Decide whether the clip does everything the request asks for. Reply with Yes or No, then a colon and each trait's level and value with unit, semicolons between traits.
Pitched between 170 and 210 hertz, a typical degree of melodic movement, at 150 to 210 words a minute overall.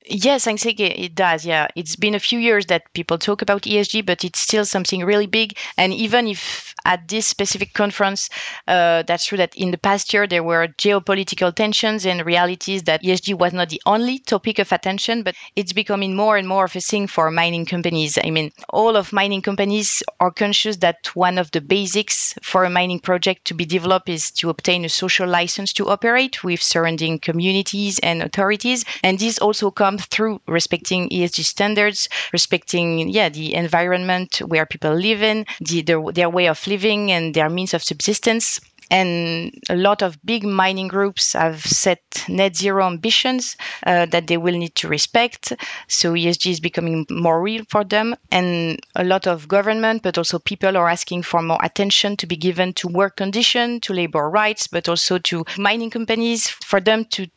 Yes: medium, 185 Hz; average, 3.1 semitones; average, 190 wpm